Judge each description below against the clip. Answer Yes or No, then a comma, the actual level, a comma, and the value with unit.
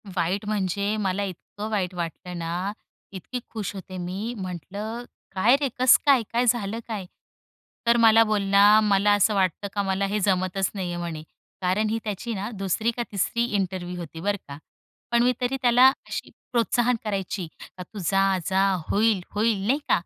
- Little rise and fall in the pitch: No, average, 3.2 semitones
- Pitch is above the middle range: Yes, high, 200 Hz